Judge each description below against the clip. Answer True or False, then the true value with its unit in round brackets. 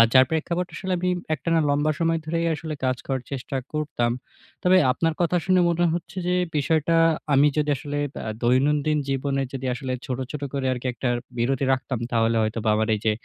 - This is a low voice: False (145 Hz)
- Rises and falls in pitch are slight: False (4.1 semitones)